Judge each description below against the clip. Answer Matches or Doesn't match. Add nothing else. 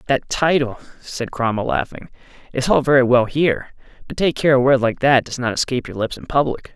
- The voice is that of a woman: Doesn't match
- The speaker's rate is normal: Doesn't match